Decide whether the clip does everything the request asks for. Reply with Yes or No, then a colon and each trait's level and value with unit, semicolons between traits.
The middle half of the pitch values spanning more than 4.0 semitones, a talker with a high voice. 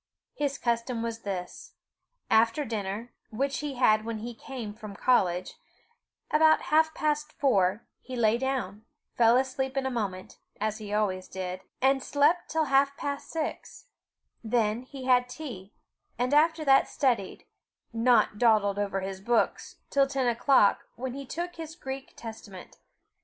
Yes: average, 4.5 semitones; high, 240 Hz